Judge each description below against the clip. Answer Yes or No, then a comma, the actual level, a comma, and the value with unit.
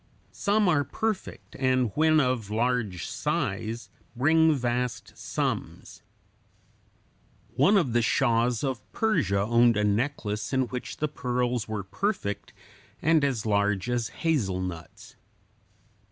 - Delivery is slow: Yes, slow, 115 wpm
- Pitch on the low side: Yes, low, 120 Hz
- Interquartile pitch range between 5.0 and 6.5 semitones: Yes, average, 5.3 semitones